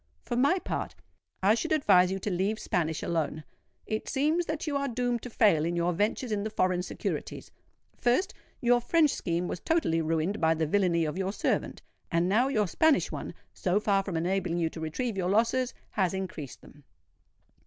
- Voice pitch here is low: No, high, 195 Hz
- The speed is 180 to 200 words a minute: Yes, average, 185 wpm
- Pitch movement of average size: No, wide, 6.2 semitones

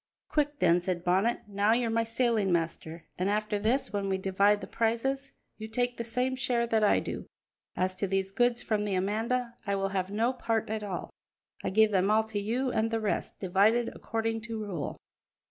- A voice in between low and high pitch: No, high, 215 Hz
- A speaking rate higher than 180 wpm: Yes, average, 200 wpm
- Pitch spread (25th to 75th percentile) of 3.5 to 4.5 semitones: No, average, 3.1 semitones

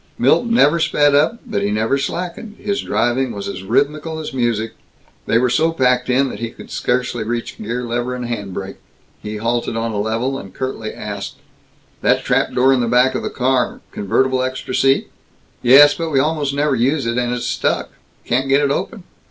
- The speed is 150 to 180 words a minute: No, average, 200 wpm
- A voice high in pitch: No, low, 125 Hz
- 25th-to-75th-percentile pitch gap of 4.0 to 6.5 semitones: No, average, 3.4 semitones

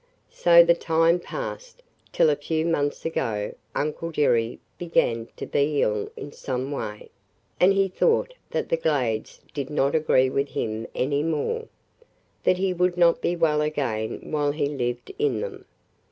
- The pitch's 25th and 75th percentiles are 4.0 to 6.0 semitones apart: Yes, average, 4.4 semitones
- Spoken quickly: No, average, 165 wpm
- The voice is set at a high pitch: No, medium, 150 Hz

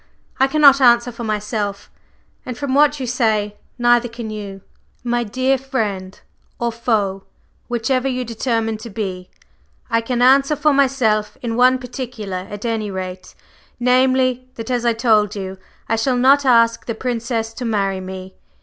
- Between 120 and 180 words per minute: Yes, average, 160 wpm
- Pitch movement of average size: Yes, average, 3.2 semitones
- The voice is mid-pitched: No, high, 235 Hz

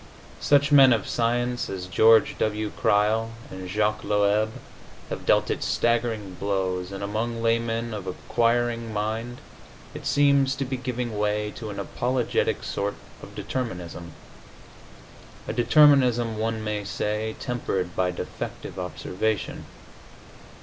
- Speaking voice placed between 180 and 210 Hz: No, low, 110 Hz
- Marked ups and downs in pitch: No, average, 2.8 semitones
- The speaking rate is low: Yes, slow, 125 wpm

